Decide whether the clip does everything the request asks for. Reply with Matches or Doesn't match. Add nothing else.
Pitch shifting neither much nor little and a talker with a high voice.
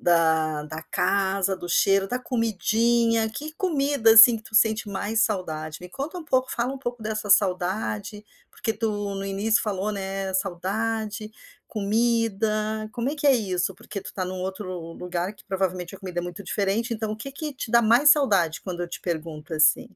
Matches